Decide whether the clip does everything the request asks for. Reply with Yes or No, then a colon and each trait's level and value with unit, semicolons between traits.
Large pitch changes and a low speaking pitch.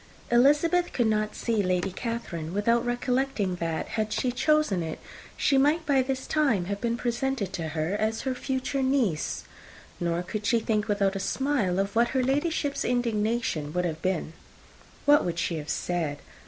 No: wide, 6.4 semitones; high, 220 Hz